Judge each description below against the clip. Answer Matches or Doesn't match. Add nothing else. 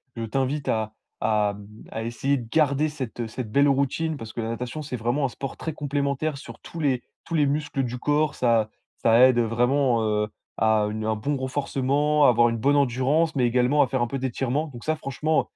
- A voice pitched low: Matches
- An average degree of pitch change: Matches